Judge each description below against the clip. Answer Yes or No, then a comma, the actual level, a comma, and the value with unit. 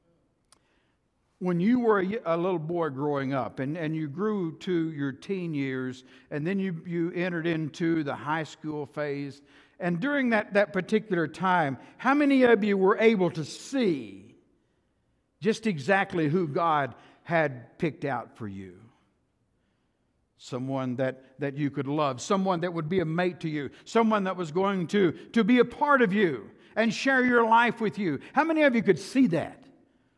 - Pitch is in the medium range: Yes, medium, 175 Hz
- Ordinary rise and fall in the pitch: No, wide, 6.1 semitones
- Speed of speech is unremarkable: Yes, average, 175 wpm